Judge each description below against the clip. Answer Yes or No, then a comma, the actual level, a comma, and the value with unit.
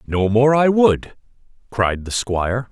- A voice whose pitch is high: No, low, 120 Hz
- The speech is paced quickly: No, average, 155 wpm